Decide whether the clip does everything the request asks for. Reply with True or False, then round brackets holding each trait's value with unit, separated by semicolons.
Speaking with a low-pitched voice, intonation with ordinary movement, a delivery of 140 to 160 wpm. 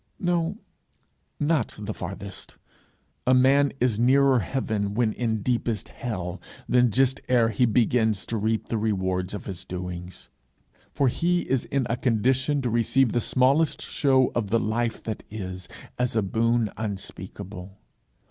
True (115 Hz; 4.2 semitones; 145 wpm)